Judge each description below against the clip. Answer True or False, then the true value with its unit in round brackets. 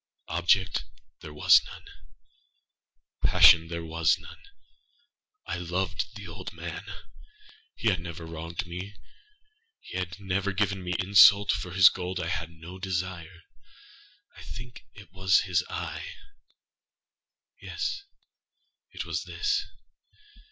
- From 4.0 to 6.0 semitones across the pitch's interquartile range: False (2.8 semitones)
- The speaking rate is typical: False (120 wpm)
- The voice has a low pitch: True (90 Hz)